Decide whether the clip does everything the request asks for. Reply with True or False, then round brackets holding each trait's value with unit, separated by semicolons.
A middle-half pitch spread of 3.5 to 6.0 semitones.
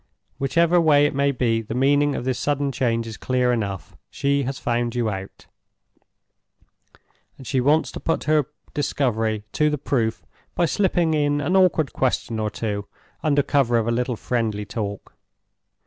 True (4.2 semitones)